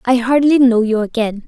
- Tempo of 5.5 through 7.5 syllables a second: No, 5.1 syllables/s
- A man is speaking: No, female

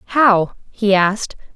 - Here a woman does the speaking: Yes, female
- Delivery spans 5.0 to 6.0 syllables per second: No, 3.3 syllables/s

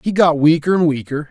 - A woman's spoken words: No, male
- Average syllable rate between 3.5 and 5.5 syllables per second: No, 5.8 syllables/s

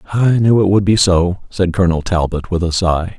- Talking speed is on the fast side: Yes, fast, 225 wpm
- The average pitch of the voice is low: Yes, very low, 90 Hz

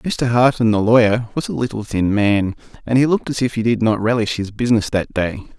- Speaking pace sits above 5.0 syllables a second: Yes, 5.7 syllables/s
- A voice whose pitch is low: Yes, low, 115 Hz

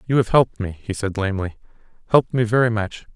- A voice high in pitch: No, low, 110 Hz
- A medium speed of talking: Yes, average, 190 wpm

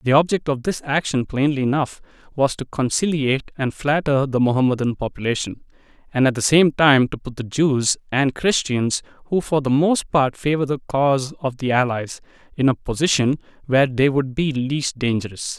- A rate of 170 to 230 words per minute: Yes, average, 175 wpm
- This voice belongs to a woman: No, male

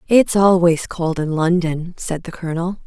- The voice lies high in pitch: No, medium, 170 Hz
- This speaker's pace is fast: No, average, 165 wpm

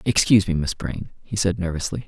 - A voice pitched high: No, very low, 95 Hz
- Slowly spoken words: No, fast, 205 wpm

